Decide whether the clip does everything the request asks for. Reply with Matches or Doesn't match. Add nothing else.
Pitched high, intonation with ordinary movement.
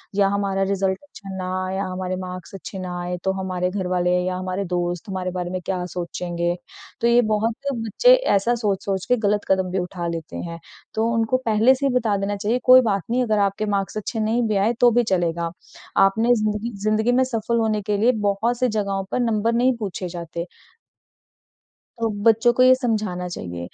Matches